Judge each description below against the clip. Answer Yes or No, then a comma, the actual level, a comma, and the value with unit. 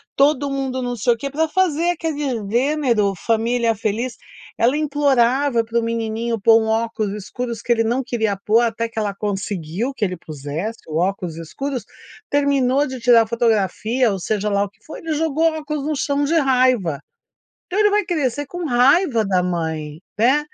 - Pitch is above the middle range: Yes, high, 235 Hz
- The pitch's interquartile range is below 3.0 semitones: No, average, 4.9 semitones